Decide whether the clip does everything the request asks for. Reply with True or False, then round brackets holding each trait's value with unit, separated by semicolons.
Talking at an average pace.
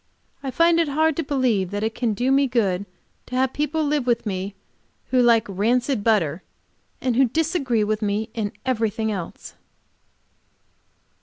True (160 wpm)